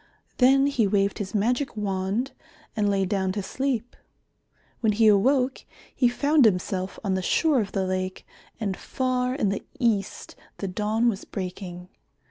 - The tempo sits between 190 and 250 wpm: No, average, 155 wpm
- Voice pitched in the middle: No, high, 210 Hz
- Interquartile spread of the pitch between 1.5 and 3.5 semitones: No, average, 4.5 semitones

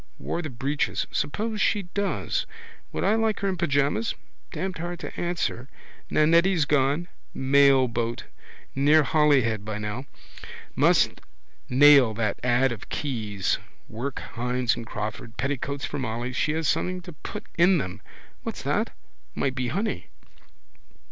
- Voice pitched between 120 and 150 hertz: Yes, medium, 140 Hz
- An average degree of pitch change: No, wide, 5.9 semitones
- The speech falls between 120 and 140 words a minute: Yes, slow, 135 wpm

